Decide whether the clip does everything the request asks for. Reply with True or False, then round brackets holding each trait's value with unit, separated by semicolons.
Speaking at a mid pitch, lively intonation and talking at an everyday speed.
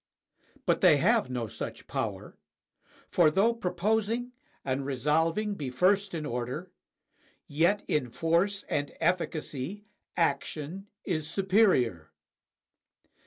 False (165 Hz; 6.1 semitones; 105 wpm)